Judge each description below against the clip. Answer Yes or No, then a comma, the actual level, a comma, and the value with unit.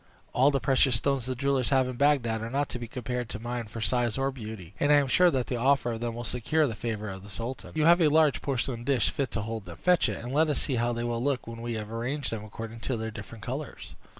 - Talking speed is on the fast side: Yes, fast, 280 wpm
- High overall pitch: No, low, 120 Hz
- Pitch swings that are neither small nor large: Yes, average, 3.3 semitones